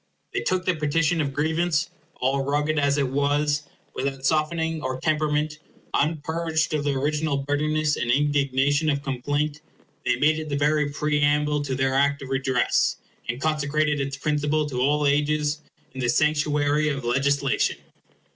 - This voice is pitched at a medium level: Yes, medium, 145 Hz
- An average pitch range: No, narrow, 1.6 semitones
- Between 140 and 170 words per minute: Yes, average, 150 wpm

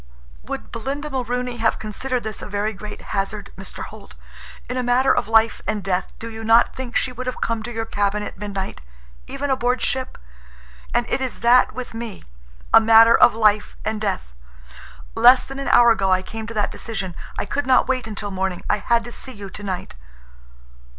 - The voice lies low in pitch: No, high, 225 Hz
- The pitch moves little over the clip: No, average, 3.7 semitones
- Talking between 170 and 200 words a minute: Yes, average, 190 wpm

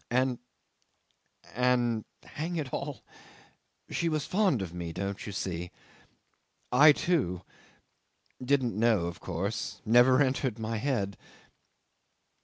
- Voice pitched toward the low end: Yes, low, 120 Hz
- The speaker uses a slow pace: Yes, slow, 110 wpm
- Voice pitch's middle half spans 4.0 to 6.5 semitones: Yes, wide, 5.6 semitones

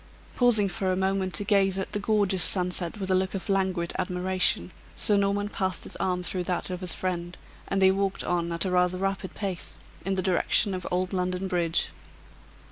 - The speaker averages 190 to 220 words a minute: Yes, average, 200 wpm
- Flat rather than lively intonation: Yes, narrow, 1.4 semitones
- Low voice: No, medium, 185 Hz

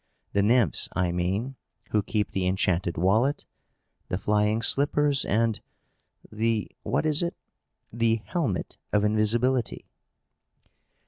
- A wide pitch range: No, average, 4.1 semitones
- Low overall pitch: Yes, low, 110 Hz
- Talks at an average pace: No, slow, 115 wpm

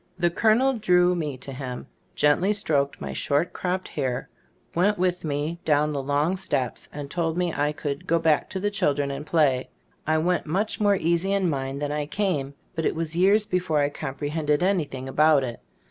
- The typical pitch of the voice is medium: Yes, medium, 160 Hz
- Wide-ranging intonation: No, average, 4.0 semitones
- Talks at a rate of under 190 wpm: No, average, 195 wpm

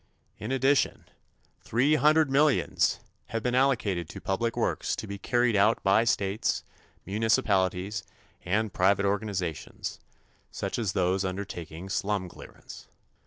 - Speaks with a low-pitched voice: Yes, low, 105 Hz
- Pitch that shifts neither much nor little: Yes, average, 4.0 semitones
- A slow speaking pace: Yes, slow, 120 wpm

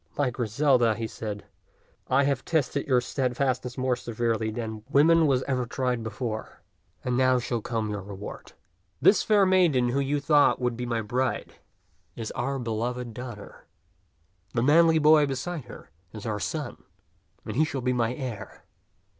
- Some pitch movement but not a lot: Yes, average, 3.3 semitones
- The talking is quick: No, average, 165 wpm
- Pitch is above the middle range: No, low, 125 Hz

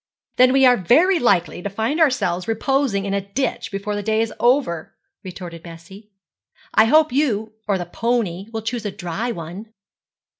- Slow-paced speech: No, average, 175 wpm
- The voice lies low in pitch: No, high, 215 Hz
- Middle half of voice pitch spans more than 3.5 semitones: Yes, average, 4.7 semitones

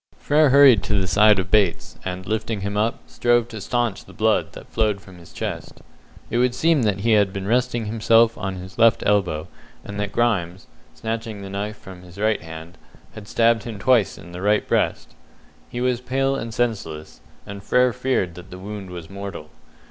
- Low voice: Yes, low, 105 Hz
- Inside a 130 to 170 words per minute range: No, average, 195 wpm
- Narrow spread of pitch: No, average, 3.7 semitones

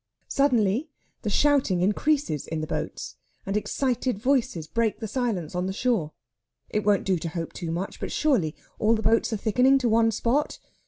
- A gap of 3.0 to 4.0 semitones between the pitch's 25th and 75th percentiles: No, wide, 5.4 semitones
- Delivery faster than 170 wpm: Yes, average, 180 wpm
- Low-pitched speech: No, high, 215 Hz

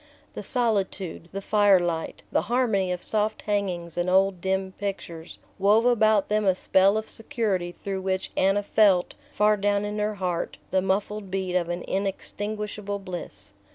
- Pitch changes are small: Yes, narrow, 2.2 semitones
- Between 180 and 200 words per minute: No, average, 160 wpm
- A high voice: Yes, high, 195 Hz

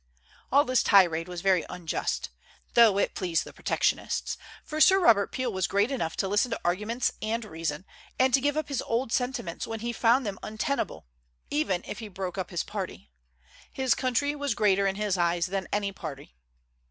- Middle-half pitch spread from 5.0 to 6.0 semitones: Yes, wide, 5.6 semitones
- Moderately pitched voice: No, high, 205 Hz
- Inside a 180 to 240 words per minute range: Yes, average, 185 wpm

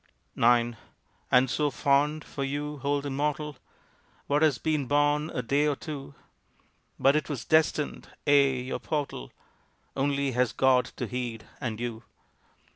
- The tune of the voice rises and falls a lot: No, average, 2.8 semitones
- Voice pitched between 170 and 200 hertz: No, medium, 140 Hz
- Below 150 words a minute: Yes, average, 140 wpm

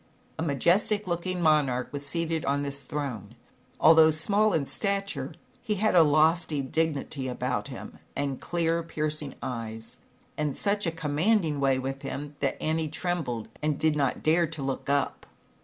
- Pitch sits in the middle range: Yes, medium, 155 Hz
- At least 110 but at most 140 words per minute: No, average, 155 wpm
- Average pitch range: Yes, average, 3.4 semitones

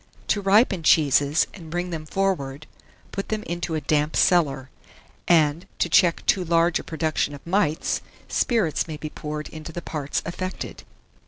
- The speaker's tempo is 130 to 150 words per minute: No, average, 160 wpm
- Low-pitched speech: No, medium, 165 Hz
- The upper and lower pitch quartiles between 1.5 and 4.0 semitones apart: Yes, average, 2.9 semitones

